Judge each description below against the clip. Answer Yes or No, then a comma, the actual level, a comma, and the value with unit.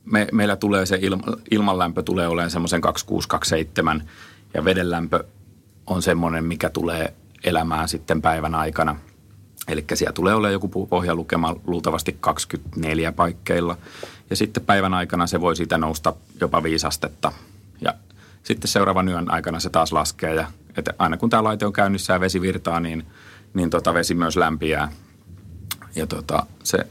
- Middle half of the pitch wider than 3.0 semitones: Yes, average, 3.5 semitones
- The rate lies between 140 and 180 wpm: Yes, average, 150 wpm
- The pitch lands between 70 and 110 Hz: Yes, very low, 90 Hz